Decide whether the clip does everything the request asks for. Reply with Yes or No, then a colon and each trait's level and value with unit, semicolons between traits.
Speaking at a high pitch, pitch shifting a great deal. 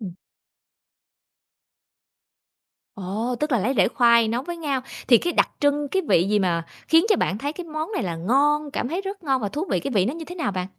Yes: very high, 265 Hz; wide, 6.9 semitones